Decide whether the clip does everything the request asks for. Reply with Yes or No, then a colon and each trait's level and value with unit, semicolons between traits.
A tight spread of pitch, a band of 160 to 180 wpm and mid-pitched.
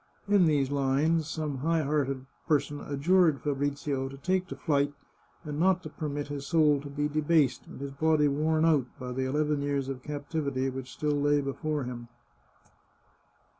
Yes: narrow, 2.1 semitones; average, 170 wpm; medium, 145 Hz